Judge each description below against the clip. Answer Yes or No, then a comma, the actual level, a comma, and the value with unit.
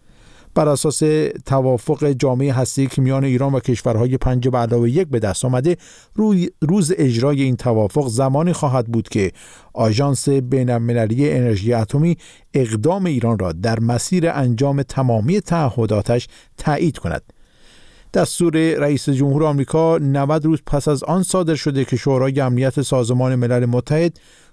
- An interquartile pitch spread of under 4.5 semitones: Yes, average, 3.9 semitones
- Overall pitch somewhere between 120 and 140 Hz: Yes, low, 135 Hz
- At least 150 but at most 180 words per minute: No, average, 140 wpm